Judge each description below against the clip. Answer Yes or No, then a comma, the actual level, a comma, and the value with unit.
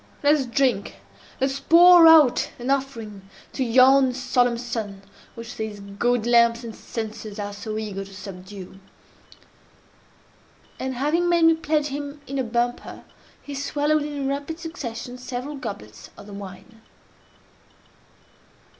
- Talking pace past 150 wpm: No, slow, 135 wpm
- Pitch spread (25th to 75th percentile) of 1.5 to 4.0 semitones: No, average, 4.8 semitones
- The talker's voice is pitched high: Yes, high, 245 Hz